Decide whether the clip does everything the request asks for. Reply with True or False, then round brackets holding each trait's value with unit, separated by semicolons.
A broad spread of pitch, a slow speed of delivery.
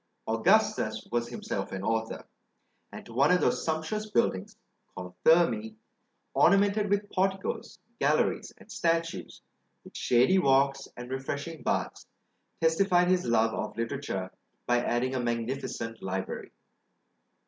True (7.2 semitones; 125 wpm)